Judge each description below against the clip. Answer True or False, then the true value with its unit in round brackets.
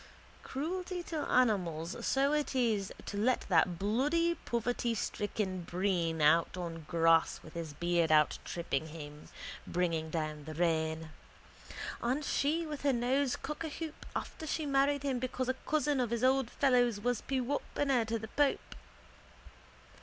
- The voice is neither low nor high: False (235 Hz)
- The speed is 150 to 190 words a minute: False (140 wpm)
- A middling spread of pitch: False (8.5 semitones)